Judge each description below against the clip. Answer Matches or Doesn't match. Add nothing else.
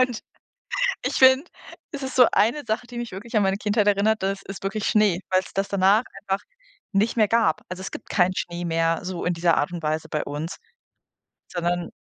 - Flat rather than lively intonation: Doesn't match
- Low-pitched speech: Doesn't match